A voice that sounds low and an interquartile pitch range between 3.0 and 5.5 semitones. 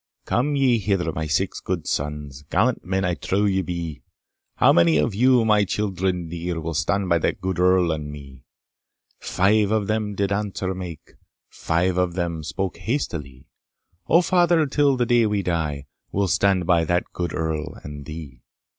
Yes: very low, 90 Hz; average, 4.2 semitones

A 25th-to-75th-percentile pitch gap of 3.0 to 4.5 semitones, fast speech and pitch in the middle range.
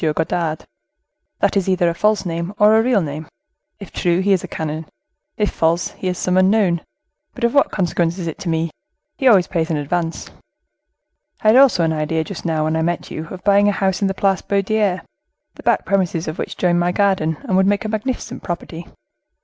Yes: average, 3.5 semitones; fast, 215 wpm; medium, 180 Hz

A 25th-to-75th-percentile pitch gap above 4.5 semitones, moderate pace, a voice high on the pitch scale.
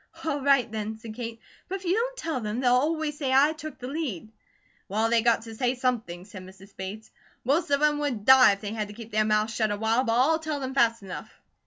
No: average, 4.9 semitones; fast, 240 wpm; high, 240 Hz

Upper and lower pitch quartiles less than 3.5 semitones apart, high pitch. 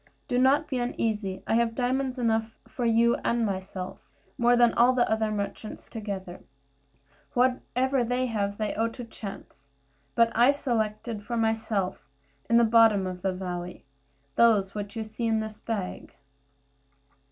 Yes: average, 2.9 semitones; high, 225 Hz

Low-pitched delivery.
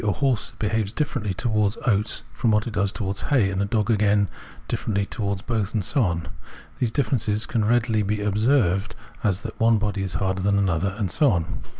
Yes: low, 105 Hz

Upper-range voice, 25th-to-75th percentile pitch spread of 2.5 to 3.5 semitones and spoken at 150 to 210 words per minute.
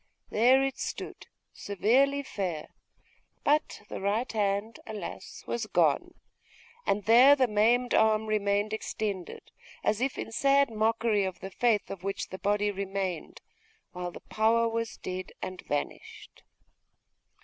No: high, 215 Hz; average, 2.8 semitones; slow, 135 wpm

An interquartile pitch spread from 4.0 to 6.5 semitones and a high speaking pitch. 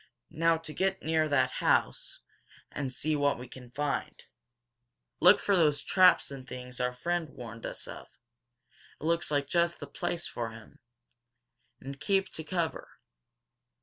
No: average, 4.7 semitones; medium, 150 Hz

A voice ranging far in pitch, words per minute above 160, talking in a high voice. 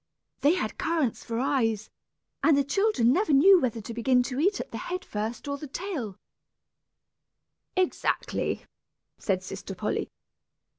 No: wide, 6.8 semitones; average, 150 wpm; very high, 265 Hz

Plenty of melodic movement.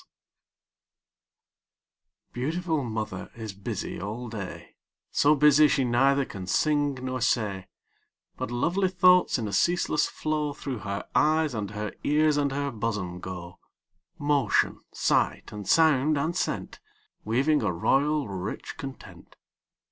Yes: wide, 6.2 semitones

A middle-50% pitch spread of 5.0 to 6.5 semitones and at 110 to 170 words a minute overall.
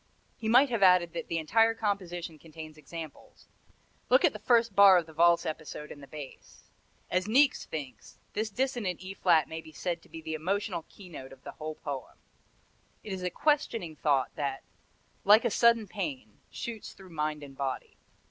No: average, 5.3 semitones; average, 185 wpm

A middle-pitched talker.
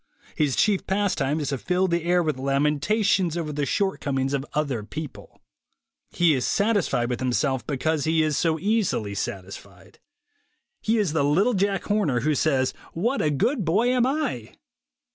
Yes: medium, 155 Hz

